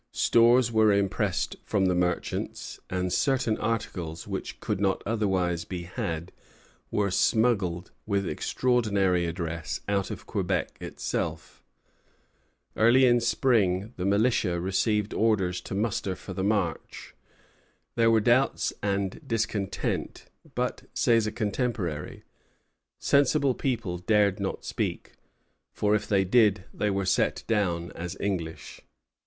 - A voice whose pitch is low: Yes, low, 100 Hz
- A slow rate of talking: Yes, slow, 125 wpm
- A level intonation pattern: No, average, 3.9 semitones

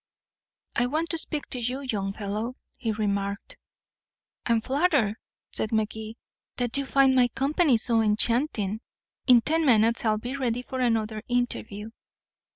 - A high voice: Yes, high, 235 Hz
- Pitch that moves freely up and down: No, average, 3.4 semitones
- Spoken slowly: No, average, 145 wpm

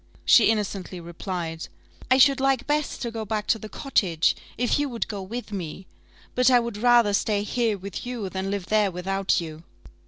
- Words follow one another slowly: No, average, 190 wpm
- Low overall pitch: No, high, 210 Hz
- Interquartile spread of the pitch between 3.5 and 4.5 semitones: Yes, average, 4.2 semitones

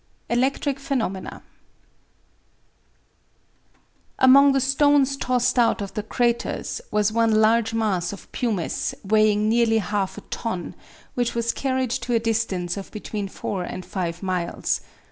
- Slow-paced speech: Yes, slow, 130 wpm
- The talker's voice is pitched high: Yes, high, 225 Hz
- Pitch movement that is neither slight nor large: Yes, average, 3.6 semitones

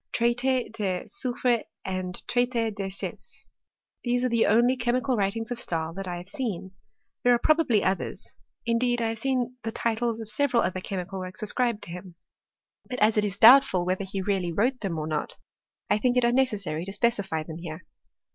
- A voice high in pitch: Yes, high, 220 Hz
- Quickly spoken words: No, average, 195 wpm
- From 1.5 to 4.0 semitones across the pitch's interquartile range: No, average, 4.6 semitones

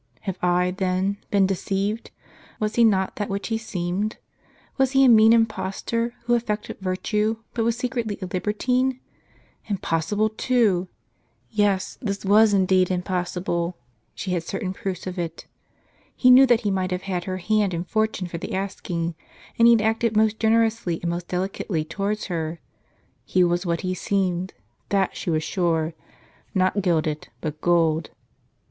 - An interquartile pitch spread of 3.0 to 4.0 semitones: Yes, average, 3.5 semitones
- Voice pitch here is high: Yes, high, 195 Hz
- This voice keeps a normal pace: Yes, average, 165 wpm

